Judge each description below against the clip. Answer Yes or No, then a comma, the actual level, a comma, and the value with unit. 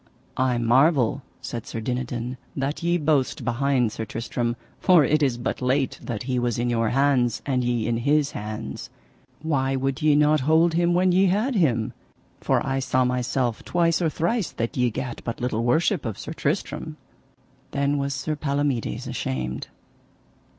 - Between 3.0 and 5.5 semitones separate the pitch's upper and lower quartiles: Yes, average, 4.2 semitones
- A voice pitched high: No, low, 135 Hz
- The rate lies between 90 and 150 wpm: No, average, 170 wpm